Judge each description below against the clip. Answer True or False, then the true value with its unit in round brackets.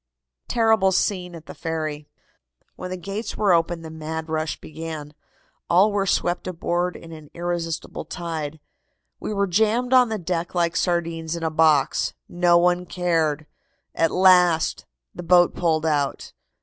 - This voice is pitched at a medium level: True (170 Hz)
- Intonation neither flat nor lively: False (2.2 semitones)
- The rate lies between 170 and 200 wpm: False (150 wpm)